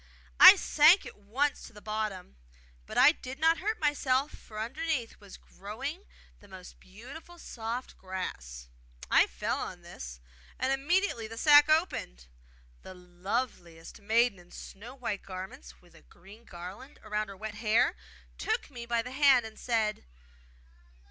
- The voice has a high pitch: Yes, high, 225 Hz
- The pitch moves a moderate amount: No, wide, 6.5 semitones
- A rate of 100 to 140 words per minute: No, average, 150 wpm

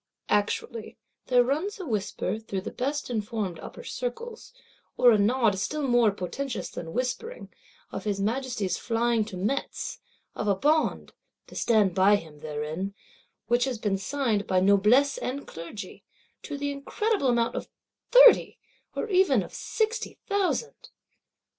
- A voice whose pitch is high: Yes, high, 235 Hz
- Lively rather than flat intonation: Yes, wide, 5.9 semitones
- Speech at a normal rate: Yes, average, 145 wpm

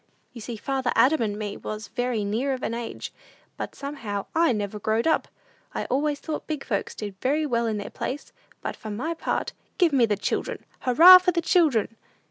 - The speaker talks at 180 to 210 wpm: Yes, average, 200 wpm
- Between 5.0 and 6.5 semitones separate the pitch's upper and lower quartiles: Yes, wide, 5.6 semitones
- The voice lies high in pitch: Yes, high, 245 Hz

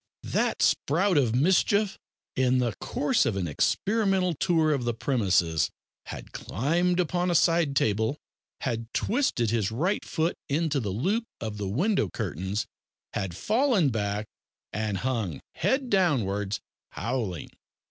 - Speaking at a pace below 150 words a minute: Yes, slow, 135 wpm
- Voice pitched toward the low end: Yes, low, 130 Hz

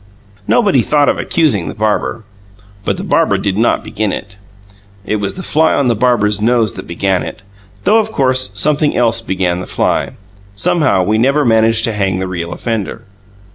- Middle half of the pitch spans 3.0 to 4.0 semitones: No, wide, 5.4 semitones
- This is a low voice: Yes, low, 110 Hz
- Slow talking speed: No, average, 180 wpm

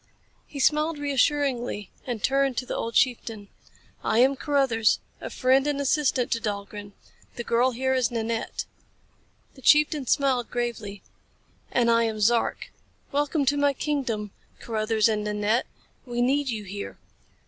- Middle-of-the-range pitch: No, high, 245 Hz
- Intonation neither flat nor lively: Yes, average, 3.7 semitones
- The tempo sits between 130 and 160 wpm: Yes, average, 145 wpm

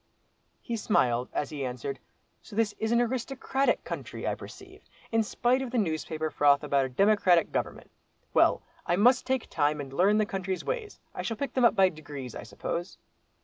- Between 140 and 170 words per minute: No, average, 190 wpm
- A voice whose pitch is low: No, high, 190 Hz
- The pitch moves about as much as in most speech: No, wide, 8.2 semitones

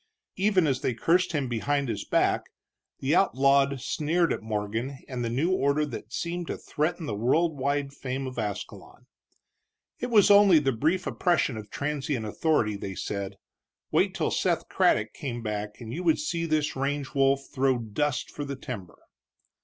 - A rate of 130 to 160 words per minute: No, average, 170 wpm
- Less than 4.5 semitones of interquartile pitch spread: No, average, 5.1 semitones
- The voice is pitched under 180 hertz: Yes, medium, 140 Hz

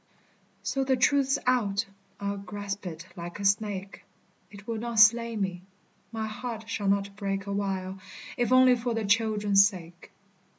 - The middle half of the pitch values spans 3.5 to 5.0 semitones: No, average, 2.7 semitones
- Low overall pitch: No, high, 205 Hz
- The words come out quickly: No, average, 155 wpm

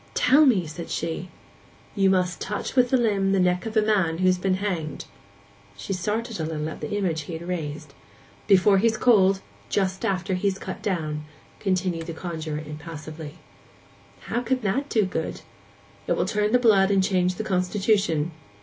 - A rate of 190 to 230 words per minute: No, average, 170 wpm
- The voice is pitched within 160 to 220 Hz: Yes, medium, 185 Hz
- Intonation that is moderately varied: Yes, average, 3.9 semitones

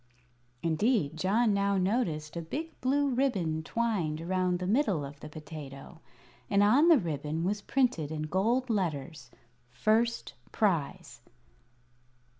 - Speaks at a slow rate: Yes, slow, 125 wpm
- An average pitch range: No, wide, 6.8 semitones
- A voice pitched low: No, medium, 185 Hz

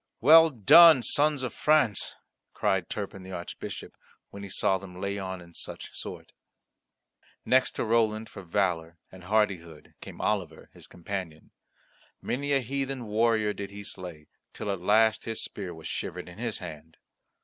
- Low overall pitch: Yes, low, 100 Hz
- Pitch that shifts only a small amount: No, average, 4.3 semitones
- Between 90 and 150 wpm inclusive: No, average, 160 wpm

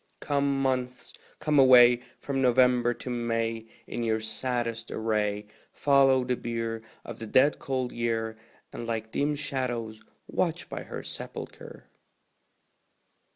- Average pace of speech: No, slow, 125 wpm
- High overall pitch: No, low, 120 Hz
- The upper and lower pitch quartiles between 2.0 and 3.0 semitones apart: Yes, narrow, 2.5 semitones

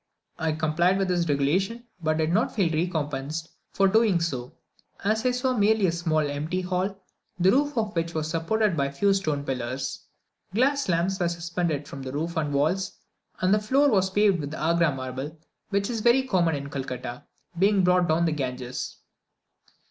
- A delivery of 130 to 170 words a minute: No, average, 180 wpm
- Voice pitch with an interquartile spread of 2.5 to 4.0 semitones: No, average, 4.7 semitones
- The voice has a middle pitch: Yes, medium, 170 Hz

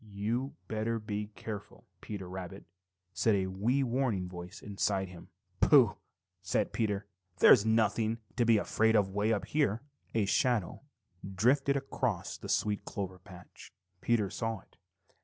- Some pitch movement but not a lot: Yes, average, 3.0 semitones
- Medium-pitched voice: No, low, 105 Hz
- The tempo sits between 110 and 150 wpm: Yes, average, 140 wpm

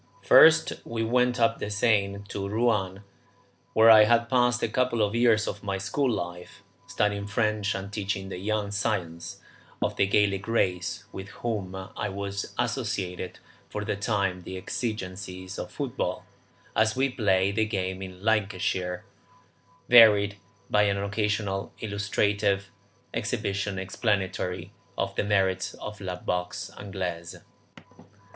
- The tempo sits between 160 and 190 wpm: No, slow, 135 wpm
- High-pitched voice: No, low, 100 Hz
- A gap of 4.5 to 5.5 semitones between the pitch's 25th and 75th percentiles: No, narrow, 2.4 semitones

